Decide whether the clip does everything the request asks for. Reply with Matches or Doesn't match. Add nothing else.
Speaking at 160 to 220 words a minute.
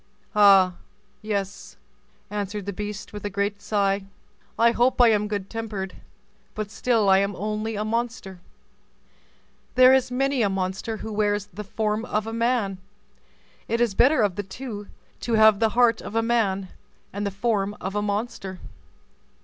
Matches